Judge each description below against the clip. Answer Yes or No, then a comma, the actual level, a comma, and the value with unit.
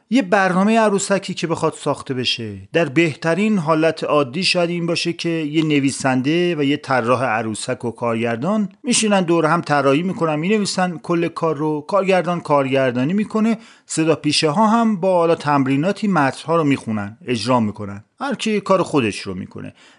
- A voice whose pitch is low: No, medium, 165 Hz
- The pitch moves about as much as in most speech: No, wide, 5.7 semitones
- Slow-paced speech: No, average, 165 wpm